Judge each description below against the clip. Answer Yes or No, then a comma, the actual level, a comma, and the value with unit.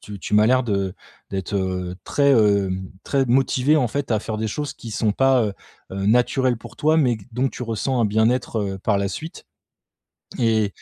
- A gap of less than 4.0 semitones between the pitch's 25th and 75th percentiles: No, average, 4.3 semitones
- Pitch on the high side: No, low, 115 Hz